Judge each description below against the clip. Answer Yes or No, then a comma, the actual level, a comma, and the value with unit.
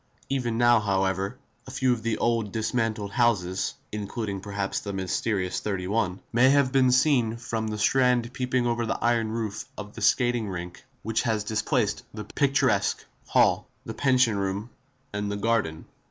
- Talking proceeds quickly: No, average, 155 wpm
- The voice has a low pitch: Yes, low, 110 Hz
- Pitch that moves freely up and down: No, average, 3.1 semitones